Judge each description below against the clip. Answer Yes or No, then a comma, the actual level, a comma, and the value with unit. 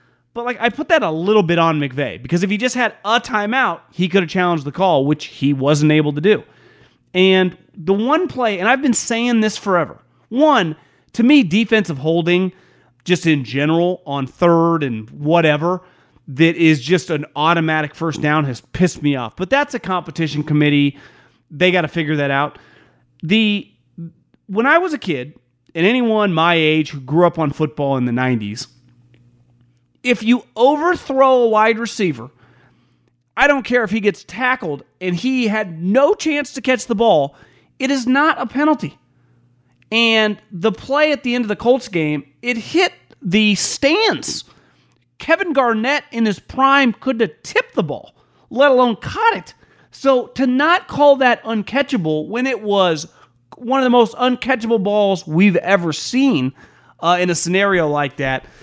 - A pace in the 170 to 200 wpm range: Yes, average, 175 wpm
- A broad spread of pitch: Yes, wide, 8.3 semitones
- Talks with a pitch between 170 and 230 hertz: Yes, medium, 185 Hz